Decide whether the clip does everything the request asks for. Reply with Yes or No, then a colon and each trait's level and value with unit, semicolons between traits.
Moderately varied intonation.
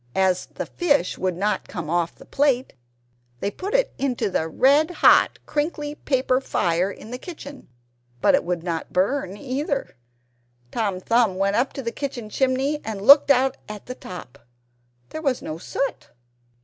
No: wide, 6.9 semitones